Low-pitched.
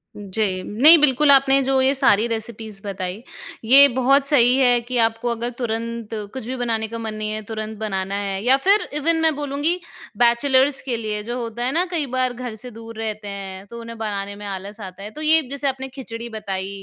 No: high, 230 Hz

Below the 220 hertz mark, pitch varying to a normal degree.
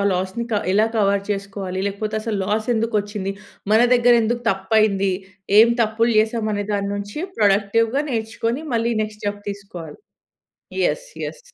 No: high, 210 Hz; narrow, 2.2 semitones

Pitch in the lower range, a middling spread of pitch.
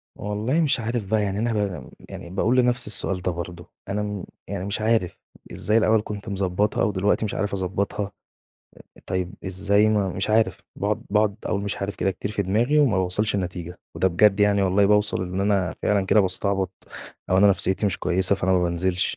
No: low, 100 Hz; narrow, 2.1 semitones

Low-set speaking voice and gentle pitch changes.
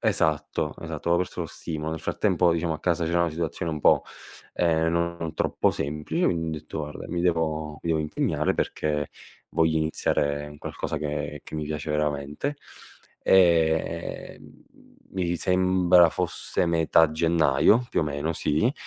Yes: very low, 80 Hz; narrow, 2.0 semitones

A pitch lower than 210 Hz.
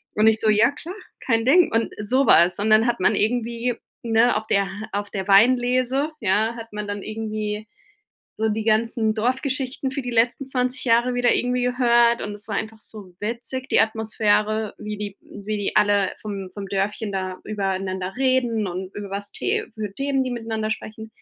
No: high, 220 Hz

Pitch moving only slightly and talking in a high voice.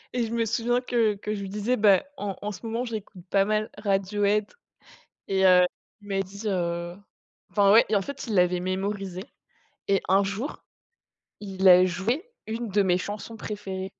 Yes: narrow, 2.3 semitones; high, 200 Hz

